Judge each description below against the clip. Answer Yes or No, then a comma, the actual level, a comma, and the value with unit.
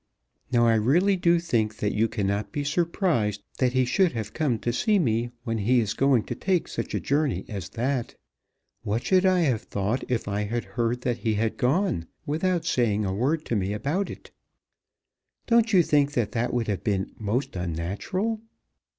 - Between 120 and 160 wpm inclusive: No, average, 190 wpm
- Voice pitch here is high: No, low, 120 Hz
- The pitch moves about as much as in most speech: No, wide, 6.8 semitones